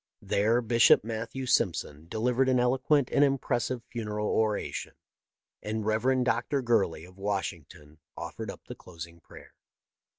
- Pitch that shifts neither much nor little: Yes, average, 4.2 semitones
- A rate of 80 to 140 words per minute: Yes, slow, 135 wpm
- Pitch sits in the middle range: No, low, 115 Hz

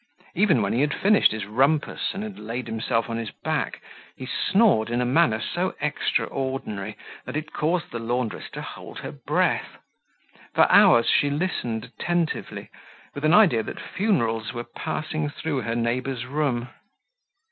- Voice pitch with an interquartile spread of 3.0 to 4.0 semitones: No, average, 5.3 semitones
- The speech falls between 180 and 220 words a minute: No, average, 160 wpm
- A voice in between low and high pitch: No, low, 130 Hz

